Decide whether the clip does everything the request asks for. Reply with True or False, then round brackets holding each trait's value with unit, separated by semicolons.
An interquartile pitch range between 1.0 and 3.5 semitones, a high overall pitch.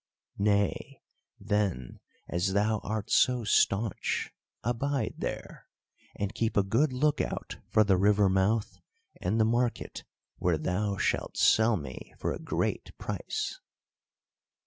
False (2.8 semitones; 105 Hz)